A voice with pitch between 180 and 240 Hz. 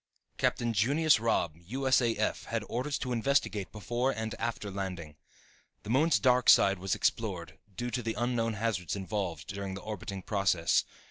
No: low, 110 Hz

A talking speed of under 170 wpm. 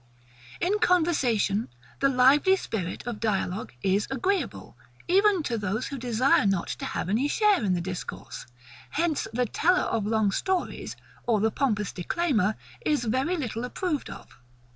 Yes: average, 150 wpm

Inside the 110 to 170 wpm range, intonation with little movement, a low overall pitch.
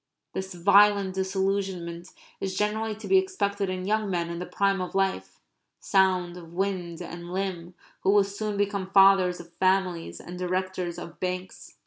No: average, 160 wpm; narrow, 1.9 semitones; high, 190 Hz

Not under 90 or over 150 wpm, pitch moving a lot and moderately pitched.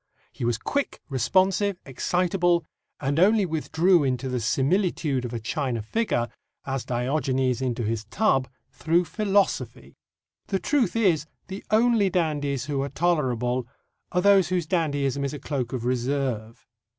Yes: average, 140 wpm; wide, 6.3 semitones; medium, 145 Hz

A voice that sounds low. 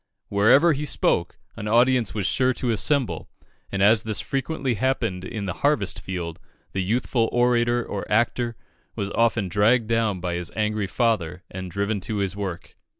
Yes: low, 110 Hz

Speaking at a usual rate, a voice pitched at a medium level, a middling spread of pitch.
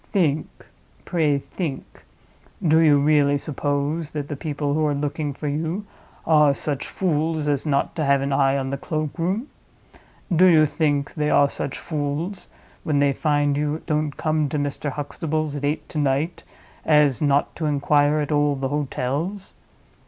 No: average, 160 wpm; medium, 150 Hz; narrow, 1.7 semitones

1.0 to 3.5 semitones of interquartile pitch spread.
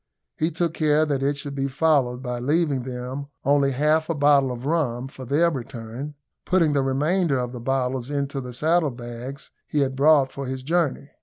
Yes: average, 2.8 semitones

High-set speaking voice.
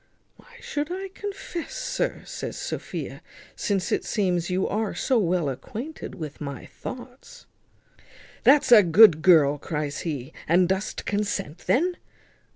Yes: high, 195 Hz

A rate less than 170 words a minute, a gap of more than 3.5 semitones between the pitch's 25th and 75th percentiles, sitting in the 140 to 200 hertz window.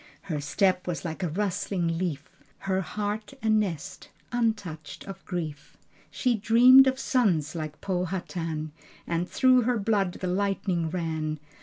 Yes: average, 140 wpm; average, 4.3 semitones; medium, 185 Hz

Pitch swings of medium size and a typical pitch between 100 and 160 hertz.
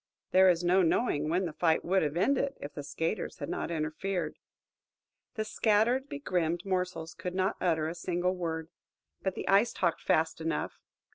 No: average, 3.1 semitones; medium, 180 Hz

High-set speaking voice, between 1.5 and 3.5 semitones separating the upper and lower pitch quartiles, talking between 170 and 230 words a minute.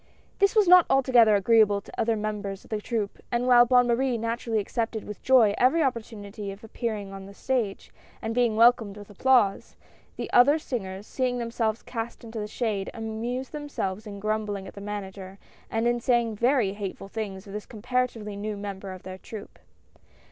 Yes: high, 220 Hz; average, 3.0 semitones; average, 185 wpm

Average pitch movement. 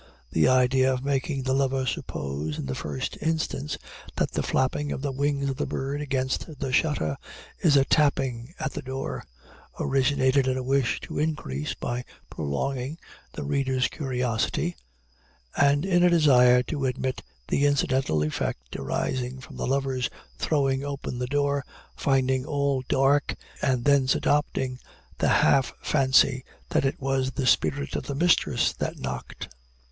No: narrow, 2.0 semitones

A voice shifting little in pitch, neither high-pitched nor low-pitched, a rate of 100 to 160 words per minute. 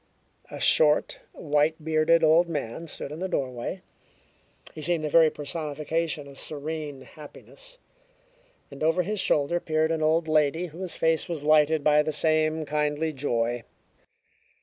Yes: narrow, 1.7 semitones; medium, 155 Hz; average, 145 wpm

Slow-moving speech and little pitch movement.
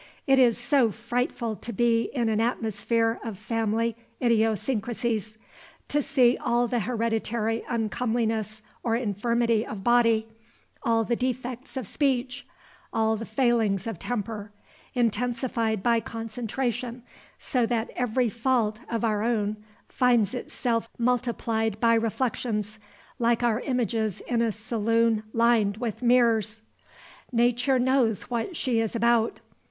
Yes: slow, 125 wpm; narrow, 1.7 semitones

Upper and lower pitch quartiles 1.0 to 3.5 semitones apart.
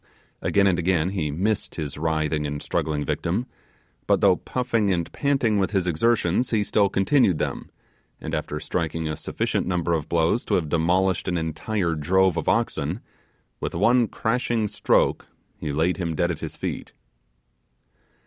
No: average, 4.5 semitones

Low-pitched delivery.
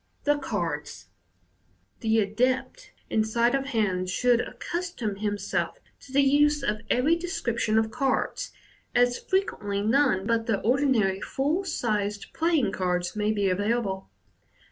No: high, 225 Hz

